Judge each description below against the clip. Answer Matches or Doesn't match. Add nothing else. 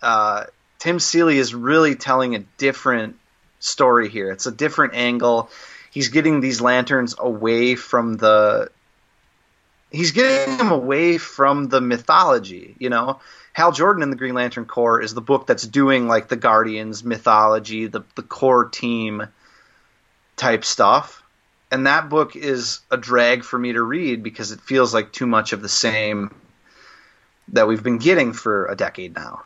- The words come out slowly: Doesn't match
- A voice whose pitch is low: Matches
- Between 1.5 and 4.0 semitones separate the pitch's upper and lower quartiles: Matches